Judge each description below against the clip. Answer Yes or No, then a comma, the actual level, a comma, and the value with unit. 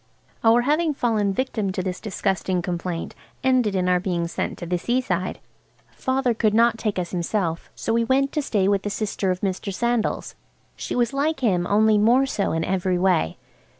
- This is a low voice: No, high, 205 Hz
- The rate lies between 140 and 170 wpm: No, average, 185 wpm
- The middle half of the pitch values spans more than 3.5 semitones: Yes, average, 4.7 semitones